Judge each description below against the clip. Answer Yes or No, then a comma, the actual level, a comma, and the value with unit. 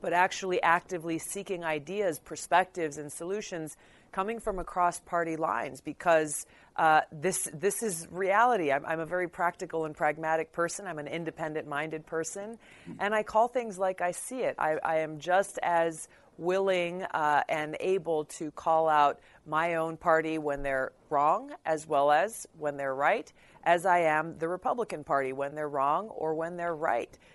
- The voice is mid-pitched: Yes, medium, 165 Hz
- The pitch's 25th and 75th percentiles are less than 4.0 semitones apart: Yes, average, 2.8 semitones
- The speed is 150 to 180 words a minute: Yes, average, 170 wpm